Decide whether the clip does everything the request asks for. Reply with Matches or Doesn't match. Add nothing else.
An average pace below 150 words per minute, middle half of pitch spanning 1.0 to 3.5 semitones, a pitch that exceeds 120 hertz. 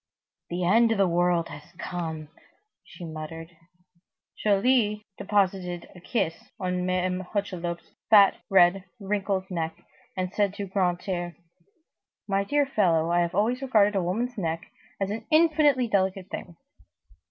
Matches